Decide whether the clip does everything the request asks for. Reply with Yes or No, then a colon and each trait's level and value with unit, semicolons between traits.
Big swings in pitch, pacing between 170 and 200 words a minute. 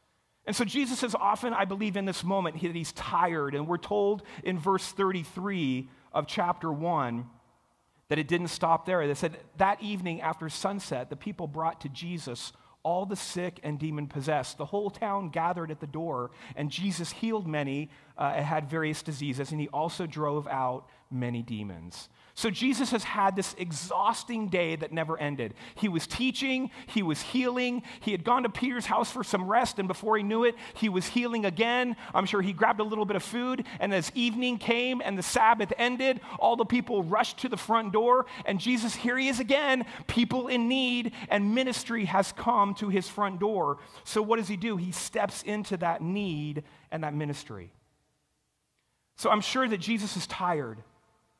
Yes: wide, 6.5 semitones; average, 190 wpm